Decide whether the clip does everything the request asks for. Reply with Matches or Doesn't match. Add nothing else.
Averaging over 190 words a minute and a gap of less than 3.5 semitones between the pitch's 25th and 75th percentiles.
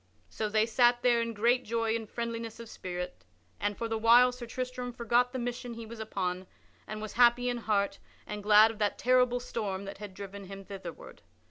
Matches